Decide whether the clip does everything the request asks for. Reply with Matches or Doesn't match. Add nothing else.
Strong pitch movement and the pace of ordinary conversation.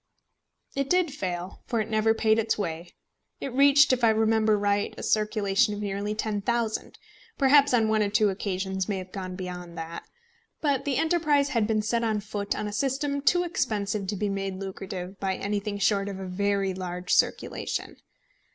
Doesn't match